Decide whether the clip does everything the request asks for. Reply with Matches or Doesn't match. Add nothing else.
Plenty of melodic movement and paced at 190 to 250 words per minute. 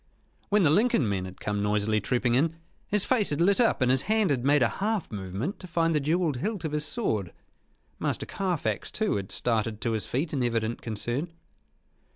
Matches